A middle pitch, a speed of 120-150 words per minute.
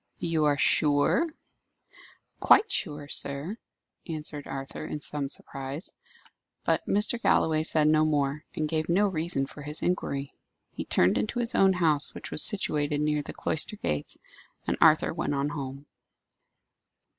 Yes: medium, 150 Hz; average, 145 wpm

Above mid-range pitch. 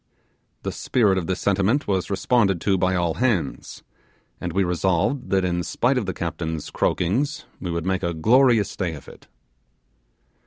No: very low, 95 Hz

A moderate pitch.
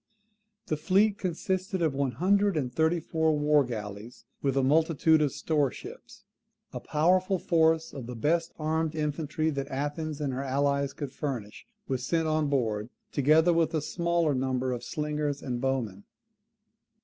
Yes: medium, 150 Hz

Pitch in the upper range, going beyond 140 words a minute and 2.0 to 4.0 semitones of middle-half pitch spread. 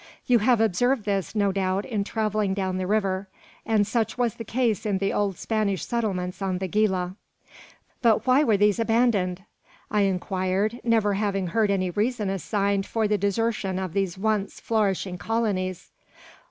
Yes: high, 205 Hz; average, 165 wpm; narrow, 2.6 semitones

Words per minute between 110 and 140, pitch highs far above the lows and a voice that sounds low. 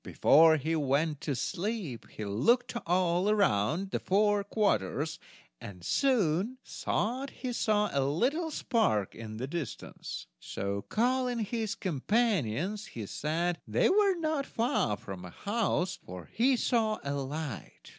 No: slow, 135 wpm; wide, 8.9 semitones; medium, 180 Hz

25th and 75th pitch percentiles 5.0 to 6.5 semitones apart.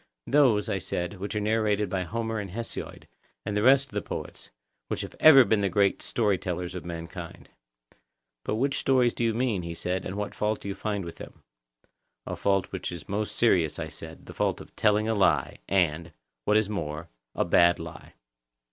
No: average, 3.8 semitones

